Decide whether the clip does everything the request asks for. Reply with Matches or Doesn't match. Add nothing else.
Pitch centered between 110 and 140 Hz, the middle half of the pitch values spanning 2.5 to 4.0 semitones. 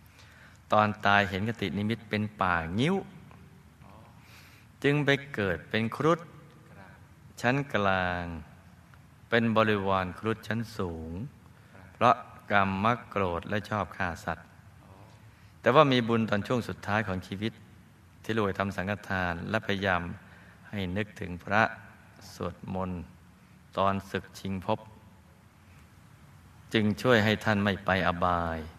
Doesn't match